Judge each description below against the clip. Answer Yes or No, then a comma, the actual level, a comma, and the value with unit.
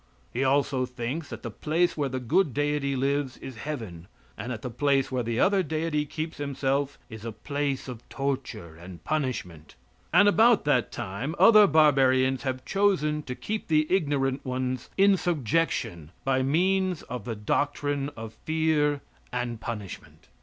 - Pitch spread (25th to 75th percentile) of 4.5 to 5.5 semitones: No, average, 3.8 semitones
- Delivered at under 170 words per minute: Yes, average, 160 wpm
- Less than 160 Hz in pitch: Yes, medium, 140 Hz